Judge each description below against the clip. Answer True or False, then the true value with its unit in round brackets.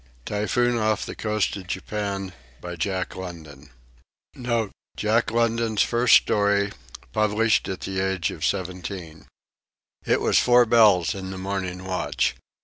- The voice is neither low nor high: False (100 Hz)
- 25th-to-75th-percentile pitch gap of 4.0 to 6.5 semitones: False (2.9 semitones)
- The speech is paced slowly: True (115 wpm)